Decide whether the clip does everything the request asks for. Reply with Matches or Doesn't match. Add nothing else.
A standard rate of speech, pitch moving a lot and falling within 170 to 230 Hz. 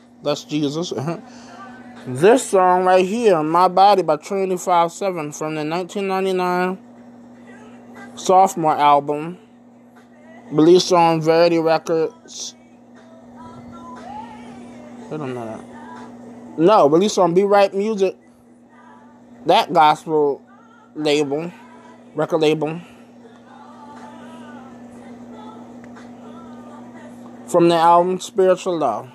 Doesn't match